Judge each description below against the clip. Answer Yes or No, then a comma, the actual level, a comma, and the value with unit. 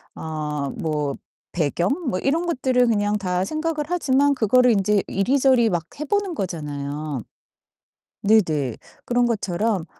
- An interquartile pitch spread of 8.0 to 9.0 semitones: Yes, wide, 8.5 semitones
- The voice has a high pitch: Yes, high, 205 Hz